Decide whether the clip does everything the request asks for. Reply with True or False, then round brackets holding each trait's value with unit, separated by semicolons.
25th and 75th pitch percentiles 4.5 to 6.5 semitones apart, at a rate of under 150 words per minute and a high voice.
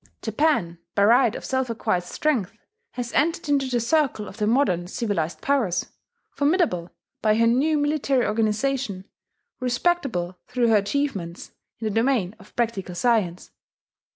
True (5.5 semitones; 140 wpm; 230 Hz)